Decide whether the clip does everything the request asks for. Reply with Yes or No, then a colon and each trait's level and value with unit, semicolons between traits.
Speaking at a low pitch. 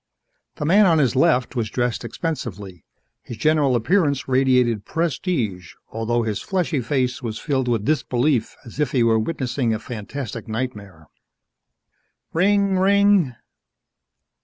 Yes: low, 130 Hz